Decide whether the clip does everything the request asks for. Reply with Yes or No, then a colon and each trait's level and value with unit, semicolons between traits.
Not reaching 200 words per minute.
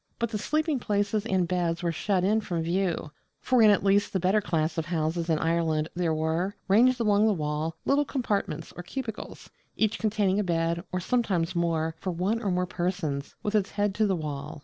No: fast, 205 wpm